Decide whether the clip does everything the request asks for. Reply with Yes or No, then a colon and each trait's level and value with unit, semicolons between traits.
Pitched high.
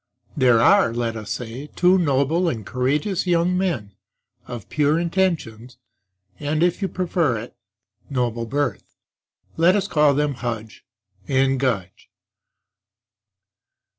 No: medium, 140 Hz